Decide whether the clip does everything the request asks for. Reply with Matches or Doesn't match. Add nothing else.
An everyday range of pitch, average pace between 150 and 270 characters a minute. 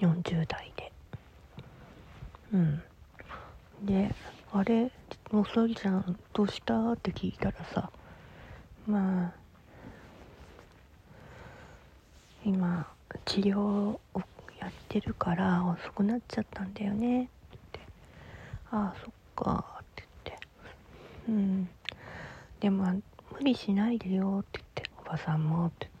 Matches